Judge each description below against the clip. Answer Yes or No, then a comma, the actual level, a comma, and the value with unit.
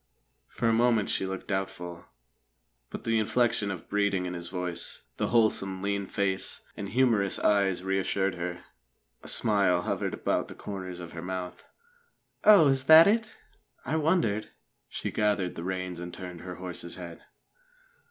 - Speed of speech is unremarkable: Yes, average, 160 wpm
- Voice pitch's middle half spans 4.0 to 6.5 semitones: No, average, 3.3 semitones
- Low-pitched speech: Yes, very low, 95 Hz